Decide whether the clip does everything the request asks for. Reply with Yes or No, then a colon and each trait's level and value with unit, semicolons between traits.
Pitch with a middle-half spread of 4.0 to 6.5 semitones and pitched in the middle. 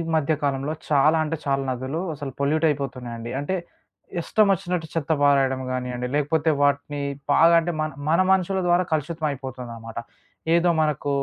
No: average, 3.3 semitones; medium, 145 Hz